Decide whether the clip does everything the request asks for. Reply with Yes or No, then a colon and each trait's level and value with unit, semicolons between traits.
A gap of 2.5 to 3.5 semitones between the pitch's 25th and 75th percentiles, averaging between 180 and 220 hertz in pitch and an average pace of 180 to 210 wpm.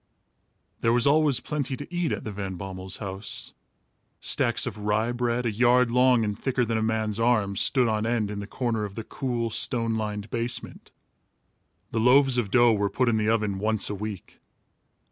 No: average, 2.8 semitones; low, 115 Hz; average, 190 wpm